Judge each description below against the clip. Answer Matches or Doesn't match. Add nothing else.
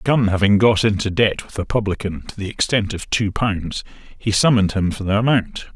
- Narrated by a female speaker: Doesn't match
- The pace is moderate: Doesn't match